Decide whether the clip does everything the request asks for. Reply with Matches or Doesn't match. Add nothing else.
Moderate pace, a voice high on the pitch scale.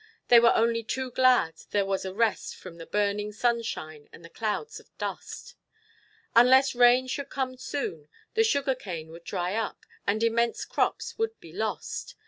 Matches